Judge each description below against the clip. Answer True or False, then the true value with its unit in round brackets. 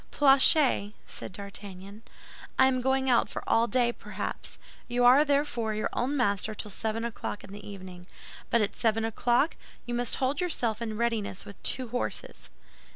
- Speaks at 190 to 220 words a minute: False (165 wpm)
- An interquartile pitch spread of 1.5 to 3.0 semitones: False (3.8 semitones)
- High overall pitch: True (235 Hz)